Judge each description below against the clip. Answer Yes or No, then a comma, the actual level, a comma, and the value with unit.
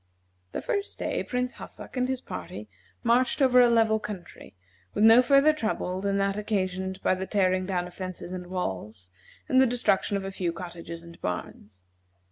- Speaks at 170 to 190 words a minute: Yes, average, 180 wpm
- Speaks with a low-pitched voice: No, high, 195 Hz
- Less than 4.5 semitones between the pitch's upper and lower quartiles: No, average, 4.9 semitones